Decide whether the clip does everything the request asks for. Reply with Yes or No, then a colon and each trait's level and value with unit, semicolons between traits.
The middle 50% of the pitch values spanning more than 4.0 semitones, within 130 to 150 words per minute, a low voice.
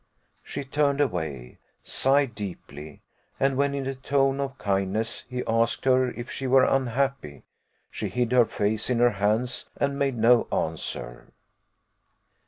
Yes: average, 4.4 semitones; average, 145 wpm; low, 125 Hz